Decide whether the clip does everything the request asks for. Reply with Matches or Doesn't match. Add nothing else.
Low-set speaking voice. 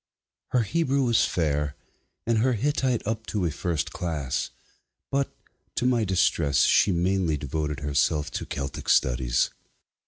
Matches